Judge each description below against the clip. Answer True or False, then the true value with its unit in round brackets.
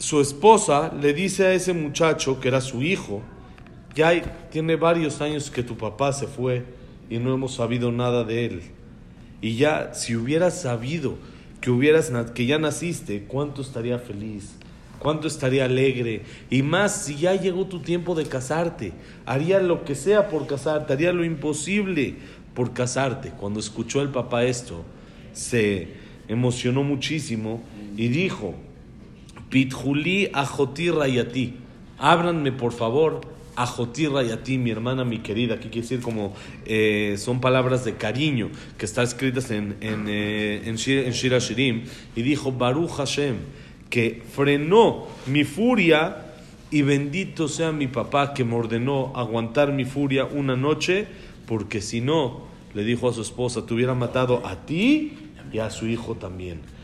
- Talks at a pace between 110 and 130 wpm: False (155 wpm)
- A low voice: True (130 Hz)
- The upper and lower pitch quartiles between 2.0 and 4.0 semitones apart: False (4.6 semitones)